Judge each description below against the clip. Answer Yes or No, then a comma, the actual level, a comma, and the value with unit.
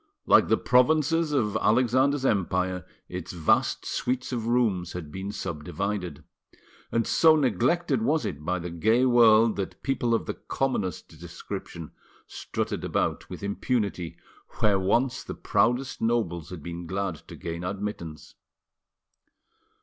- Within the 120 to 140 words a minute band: Yes, slow, 135 wpm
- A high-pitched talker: No, low, 105 Hz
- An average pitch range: No, wide, 5.9 semitones